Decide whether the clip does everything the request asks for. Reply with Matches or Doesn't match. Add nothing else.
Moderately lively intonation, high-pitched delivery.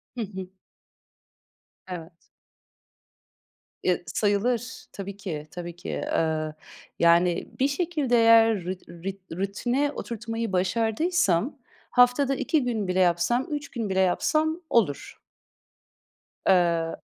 Doesn't match